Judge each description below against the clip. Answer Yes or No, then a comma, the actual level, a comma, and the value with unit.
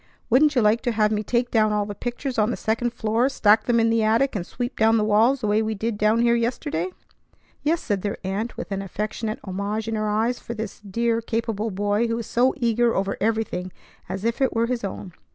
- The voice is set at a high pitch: Yes, high, 220 Hz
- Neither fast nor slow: No, fast, 235 wpm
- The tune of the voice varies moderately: No, narrow, 2.1 semitones